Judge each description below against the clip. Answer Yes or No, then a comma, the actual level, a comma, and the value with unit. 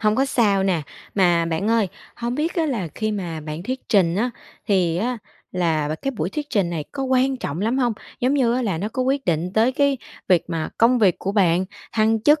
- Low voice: No, high, 215 Hz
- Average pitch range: No, wide, 6.5 semitones